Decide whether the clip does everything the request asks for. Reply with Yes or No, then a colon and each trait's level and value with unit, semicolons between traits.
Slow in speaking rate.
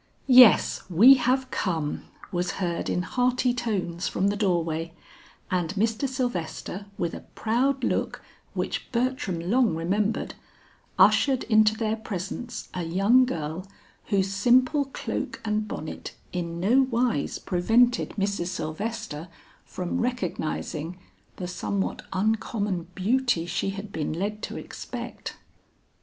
Yes: slow, 125 wpm